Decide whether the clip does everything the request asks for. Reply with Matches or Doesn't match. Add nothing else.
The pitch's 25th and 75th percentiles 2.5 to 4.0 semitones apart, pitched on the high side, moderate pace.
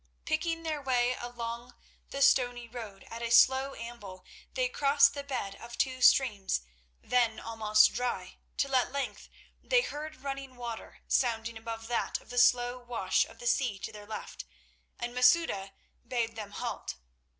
Matches